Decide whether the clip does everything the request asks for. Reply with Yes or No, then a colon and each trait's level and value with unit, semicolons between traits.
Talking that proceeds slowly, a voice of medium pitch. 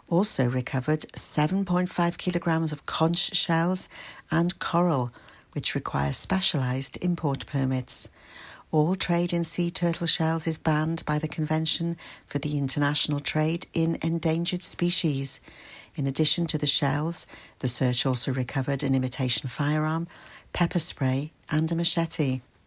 Yes: slow, 130 wpm; medium, 155 Hz